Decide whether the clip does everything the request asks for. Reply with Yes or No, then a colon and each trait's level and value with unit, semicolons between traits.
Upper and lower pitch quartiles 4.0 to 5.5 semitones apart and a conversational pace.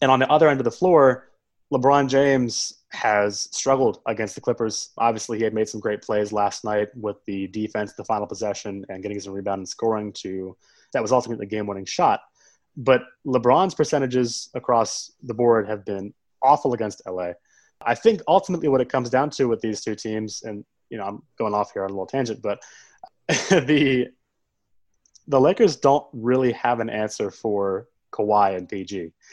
Yes: average, 4.3 semitones; average, 185 wpm